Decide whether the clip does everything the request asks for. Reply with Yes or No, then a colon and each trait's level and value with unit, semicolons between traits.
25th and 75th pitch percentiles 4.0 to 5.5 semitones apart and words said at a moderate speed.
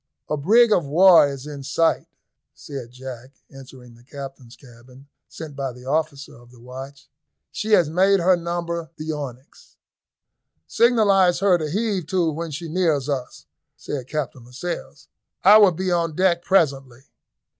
Yes: average, 4.9 semitones; average, 155 wpm